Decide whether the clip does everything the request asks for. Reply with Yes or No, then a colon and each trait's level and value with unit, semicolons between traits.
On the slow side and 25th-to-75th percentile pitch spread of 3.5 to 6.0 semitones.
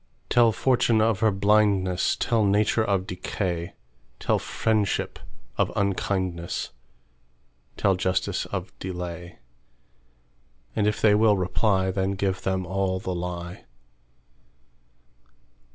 No: slow, 90 wpm; average, 3.1 semitones